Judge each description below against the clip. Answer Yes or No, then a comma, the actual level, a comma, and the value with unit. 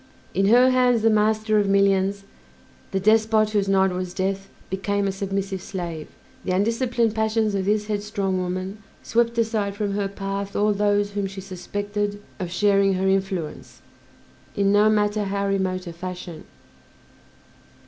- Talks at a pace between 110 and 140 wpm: No, average, 150 wpm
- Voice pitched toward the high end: Yes, high, 200 Hz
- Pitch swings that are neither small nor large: No, narrow, 1.8 semitones